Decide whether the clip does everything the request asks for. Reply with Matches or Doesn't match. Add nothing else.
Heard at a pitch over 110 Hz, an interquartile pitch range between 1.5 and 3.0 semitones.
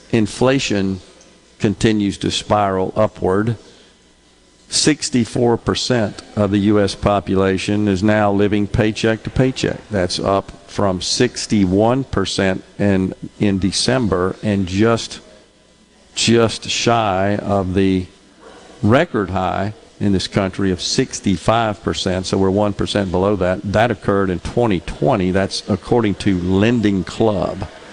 Doesn't match